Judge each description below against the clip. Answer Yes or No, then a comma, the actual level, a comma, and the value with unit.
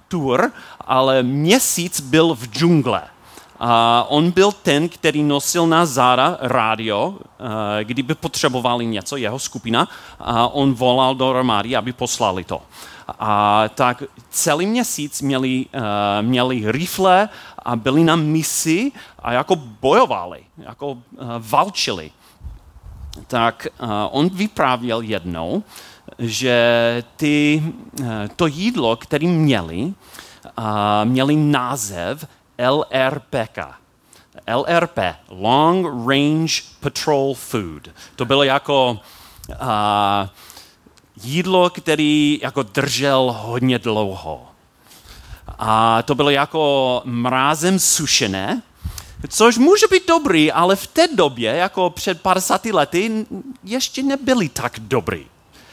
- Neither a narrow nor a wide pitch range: No, wide, 5.8 semitones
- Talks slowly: Yes, slow, 100 wpm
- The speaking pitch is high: No, low, 135 Hz